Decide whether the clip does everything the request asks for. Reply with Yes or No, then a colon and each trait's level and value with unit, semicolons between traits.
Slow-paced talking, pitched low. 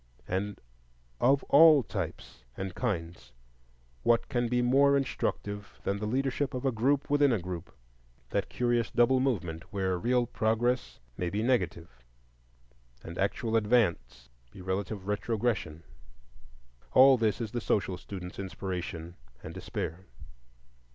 Yes: slow, 125 wpm; low, 105 Hz